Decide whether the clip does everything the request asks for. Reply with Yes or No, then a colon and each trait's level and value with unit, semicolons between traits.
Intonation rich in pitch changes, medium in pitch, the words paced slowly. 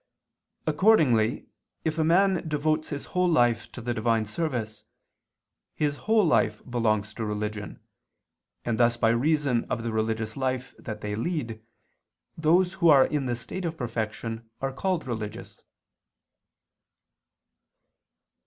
No: wide, 5.9 semitones; low, 120 Hz; slow, 130 wpm